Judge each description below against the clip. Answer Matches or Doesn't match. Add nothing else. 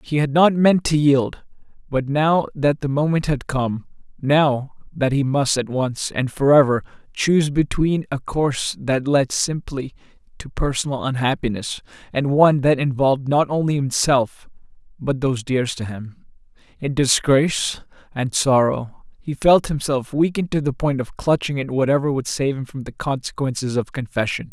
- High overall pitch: Doesn't match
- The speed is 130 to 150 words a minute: Doesn't match